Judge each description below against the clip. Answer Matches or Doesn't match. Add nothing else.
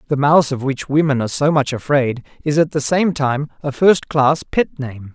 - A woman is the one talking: Doesn't match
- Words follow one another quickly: Matches